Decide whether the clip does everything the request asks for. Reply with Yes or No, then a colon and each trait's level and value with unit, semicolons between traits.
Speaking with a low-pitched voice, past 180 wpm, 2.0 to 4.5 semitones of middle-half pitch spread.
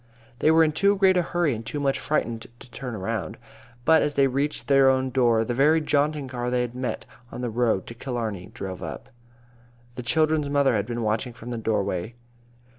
Yes: low, 125 Hz; fast, 205 wpm; average, 4.2 semitones